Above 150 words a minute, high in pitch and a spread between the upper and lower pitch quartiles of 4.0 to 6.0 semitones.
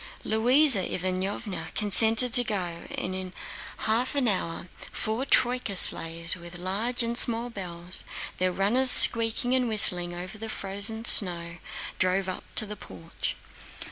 No: average, 140 wpm; high, 200 Hz; average, 4.3 semitones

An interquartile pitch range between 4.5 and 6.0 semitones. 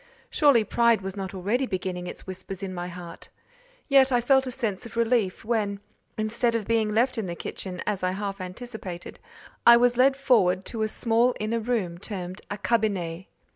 No: average, 4.1 semitones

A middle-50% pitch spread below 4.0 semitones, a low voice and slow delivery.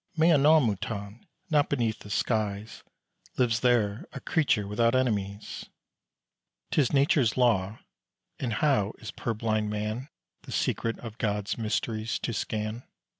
Yes: average, 3.1 semitones; low, 115 Hz; slow, 130 wpm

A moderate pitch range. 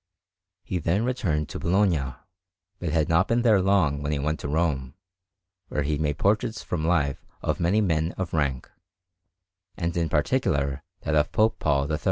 Yes: average, 4.5 semitones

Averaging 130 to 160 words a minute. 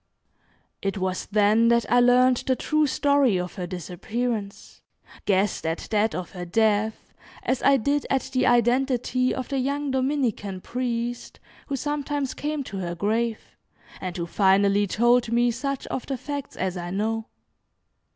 Yes: average, 155 wpm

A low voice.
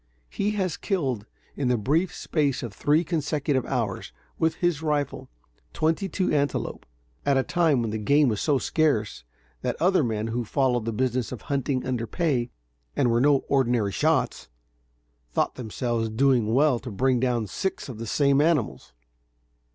Yes: low, 130 Hz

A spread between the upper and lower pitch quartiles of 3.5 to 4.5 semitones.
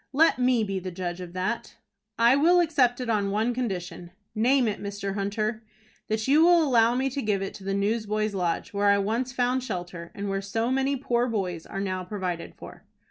Yes: average, 4.1 semitones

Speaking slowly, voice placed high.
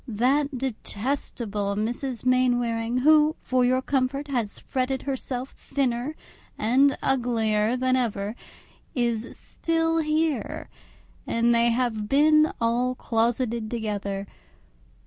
Yes: slow, 105 wpm; very high, 250 Hz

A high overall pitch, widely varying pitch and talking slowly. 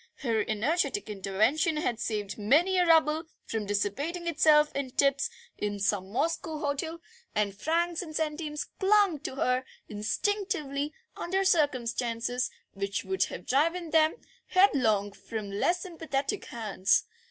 Yes: very high, 285 Hz; wide, 7.3 semitones; slow, 130 wpm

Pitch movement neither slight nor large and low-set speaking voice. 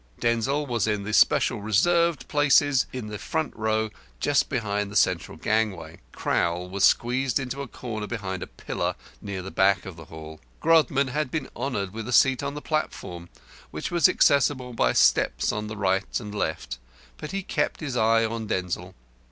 No: wide, 6.0 semitones; low, 110 Hz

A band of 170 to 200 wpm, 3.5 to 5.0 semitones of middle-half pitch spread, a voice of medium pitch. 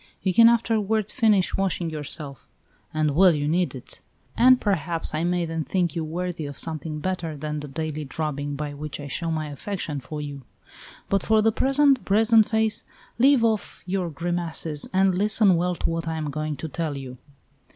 Yes: average, 185 wpm; average, 4.6 semitones; medium, 165 Hz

